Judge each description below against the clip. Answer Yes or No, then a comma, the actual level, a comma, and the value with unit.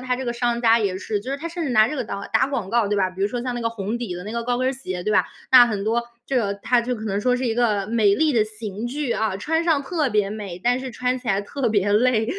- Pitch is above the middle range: Yes, high, 235 Hz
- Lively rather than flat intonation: No, average, 3.5 semitones